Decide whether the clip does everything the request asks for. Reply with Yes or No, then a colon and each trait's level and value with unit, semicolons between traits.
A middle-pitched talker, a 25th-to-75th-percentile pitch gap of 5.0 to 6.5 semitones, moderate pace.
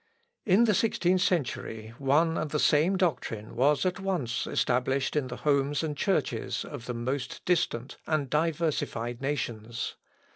Yes: medium, 145 Hz; average, 5.3 semitones; average, 145 wpm